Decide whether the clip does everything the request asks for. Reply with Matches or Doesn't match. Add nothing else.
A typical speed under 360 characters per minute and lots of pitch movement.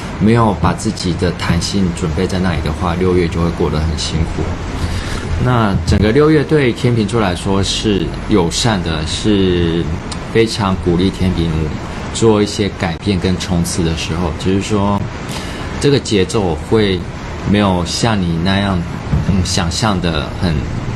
Doesn't match